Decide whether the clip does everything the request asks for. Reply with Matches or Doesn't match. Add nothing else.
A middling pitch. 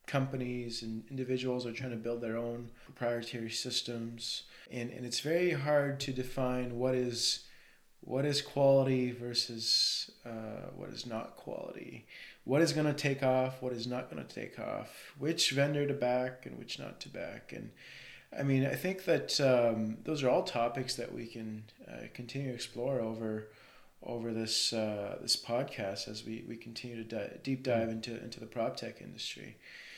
Doesn't match